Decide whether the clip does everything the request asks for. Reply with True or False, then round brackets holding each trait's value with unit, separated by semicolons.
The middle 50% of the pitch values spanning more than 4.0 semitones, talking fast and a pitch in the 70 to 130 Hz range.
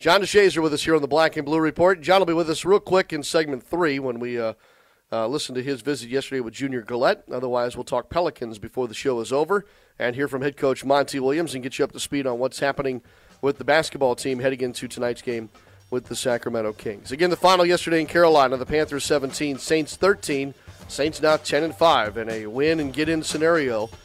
False (4.5 semitones; 230 wpm; 140 Hz)